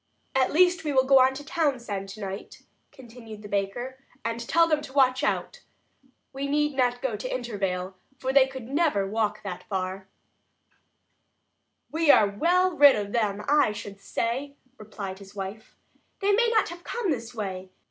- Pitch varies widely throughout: Yes, wide, 6.0 semitones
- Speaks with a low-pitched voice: No, high, 245 Hz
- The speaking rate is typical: Yes, average, 170 wpm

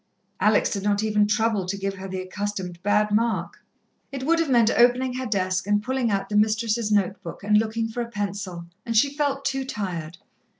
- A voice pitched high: Yes, high, 210 Hz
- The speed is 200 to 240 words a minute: Yes, fast, 205 wpm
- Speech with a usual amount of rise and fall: Yes, average, 3.0 semitones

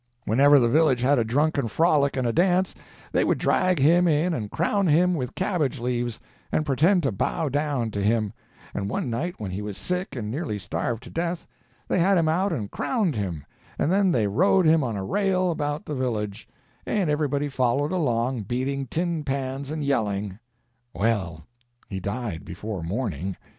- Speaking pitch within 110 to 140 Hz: Yes, low, 135 Hz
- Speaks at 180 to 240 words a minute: Yes, average, 185 wpm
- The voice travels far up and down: Yes, wide, 6.8 semitones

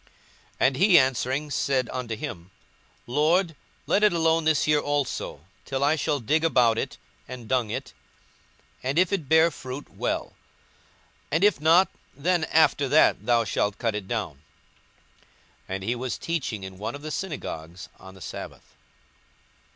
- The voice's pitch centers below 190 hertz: Yes, low, 135 Hz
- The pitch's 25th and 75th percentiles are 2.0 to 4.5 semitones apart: No, wide, 5.5 semitones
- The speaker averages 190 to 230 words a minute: No, average, 165 wpm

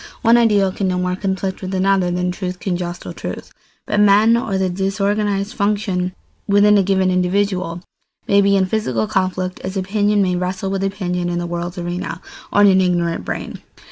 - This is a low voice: No, high, 190 Hz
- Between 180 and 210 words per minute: Yes, average, 185 wpm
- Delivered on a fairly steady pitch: Yes, narrow, 1.9 semitones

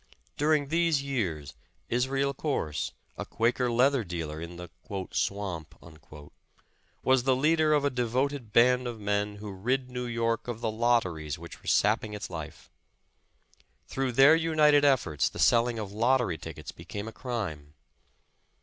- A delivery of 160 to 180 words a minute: No, average, 150 wpm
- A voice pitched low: Yes, low, 115 Hz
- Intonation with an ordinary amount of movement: No, wide, 6.3 semitones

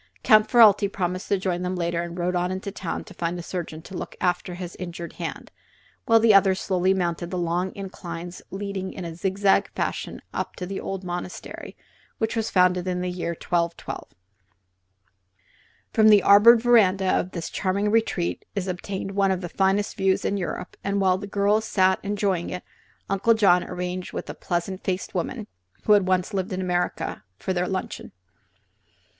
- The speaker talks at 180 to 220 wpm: Yes, average, 185 wpm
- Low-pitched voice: No, medium, 185 Hz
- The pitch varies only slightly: Yes, narrow, 2.0 semitones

